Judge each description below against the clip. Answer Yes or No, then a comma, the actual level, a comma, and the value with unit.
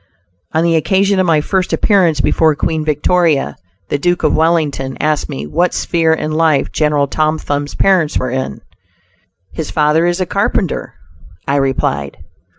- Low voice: No, medium, 155 Hz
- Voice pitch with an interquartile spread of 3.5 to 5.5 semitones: No, average, 3.1 semitones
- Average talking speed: Yes, average, 155 wpm